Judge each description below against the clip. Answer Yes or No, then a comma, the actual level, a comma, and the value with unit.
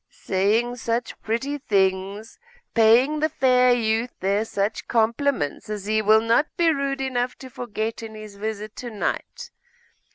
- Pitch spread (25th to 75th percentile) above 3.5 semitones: No, average, 2.9 semitones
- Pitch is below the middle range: No, high, 225 Hz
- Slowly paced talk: No, average, 150 wpm